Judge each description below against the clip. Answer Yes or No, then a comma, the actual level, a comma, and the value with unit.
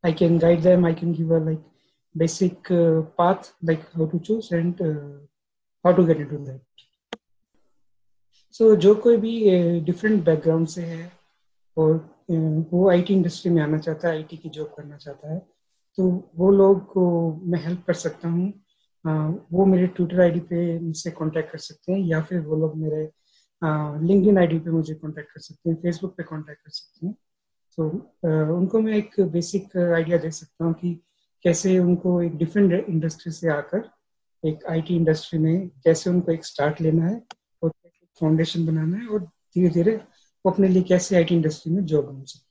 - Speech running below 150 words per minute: Yes, average, 140 wpm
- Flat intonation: Yes, narrow, 2.3 semitones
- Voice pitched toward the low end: No, medium, 170 Hz